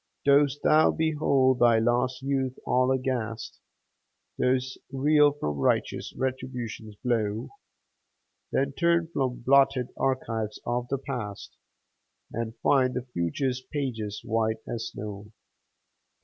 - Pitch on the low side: Yes, low, 130 Hz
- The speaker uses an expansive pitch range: No, average, 3.2 semitones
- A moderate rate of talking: No, slow, 110 wpm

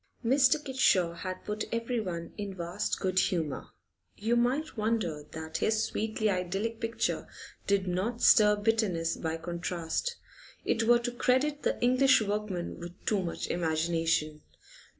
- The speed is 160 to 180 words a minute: No, slow, 135 wpm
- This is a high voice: Yes, high, 205 Hz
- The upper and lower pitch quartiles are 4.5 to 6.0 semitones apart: Yes, average, 5.1 semitones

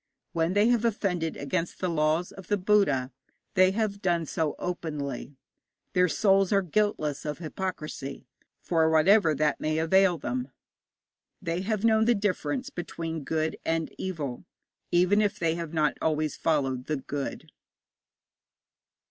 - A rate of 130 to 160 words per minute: Yes, average, 140 wpm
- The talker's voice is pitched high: No, medium, 165 Hz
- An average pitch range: Yes, average, 4.2 semitones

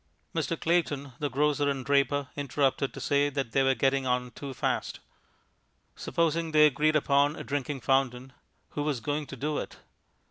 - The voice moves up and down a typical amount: No, narrow, 1.9 semitones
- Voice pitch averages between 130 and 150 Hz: Yes, medium, 140 Hz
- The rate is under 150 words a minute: No, average, 170 wpm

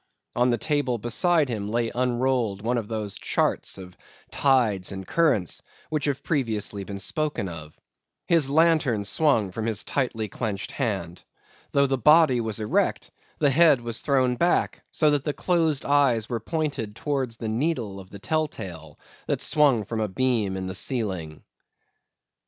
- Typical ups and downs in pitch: No, wide, 5.7 semitones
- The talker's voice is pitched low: Yes, low, 120 Hz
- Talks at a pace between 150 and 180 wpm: Yes, average, 165 wpm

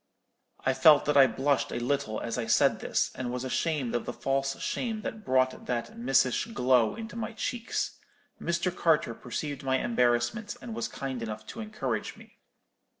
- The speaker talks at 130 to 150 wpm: No, average, 175 wpm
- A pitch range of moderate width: No, wide, 5.9 semitones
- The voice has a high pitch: No, low, 135 Hz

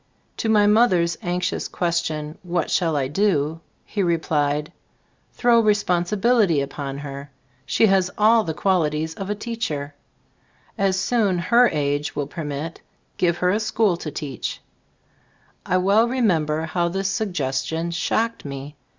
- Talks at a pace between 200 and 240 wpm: No, average, 150 wpm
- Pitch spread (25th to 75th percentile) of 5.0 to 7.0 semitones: Yes, wide, 5.5 semitones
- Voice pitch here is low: No, medium, 175 Hz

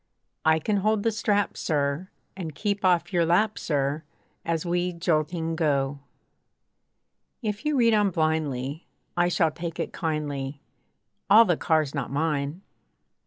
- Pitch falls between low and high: Yes, medium, 165 Hz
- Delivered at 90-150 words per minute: Yes, average, 140 wpm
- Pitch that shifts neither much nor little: Yes, average, 4.2 semitones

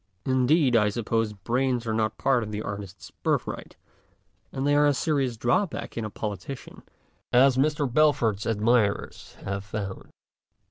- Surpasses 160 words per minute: No, average, 145 wpm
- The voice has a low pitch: Yes, low, 120 Hz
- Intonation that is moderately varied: Yes, average, 4.2 semitones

